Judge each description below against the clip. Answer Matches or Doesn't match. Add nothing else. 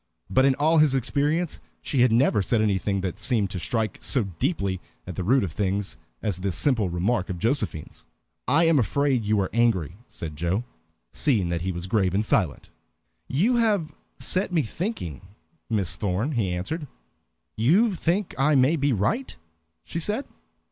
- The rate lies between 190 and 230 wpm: Doesn't match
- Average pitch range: Doesn't match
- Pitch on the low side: Matches